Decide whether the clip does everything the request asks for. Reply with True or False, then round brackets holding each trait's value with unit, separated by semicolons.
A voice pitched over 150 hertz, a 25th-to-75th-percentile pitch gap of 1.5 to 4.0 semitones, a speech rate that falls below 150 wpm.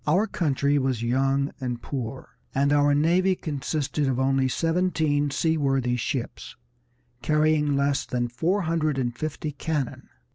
False (145 Hz; 2.8 semitones; 135 wpm)